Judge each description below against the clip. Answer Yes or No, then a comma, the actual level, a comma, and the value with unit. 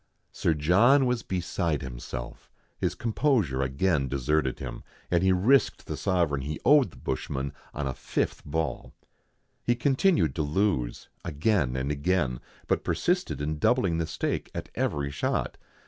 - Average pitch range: No, wide, 6.6 semitones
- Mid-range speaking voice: No, very low, 80 Hz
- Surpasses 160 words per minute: No, average, 145 wpm